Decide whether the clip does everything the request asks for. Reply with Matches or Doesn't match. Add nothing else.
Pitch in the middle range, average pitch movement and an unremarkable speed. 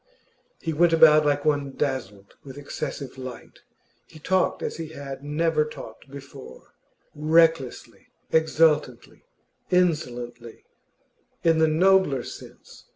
Doesn't match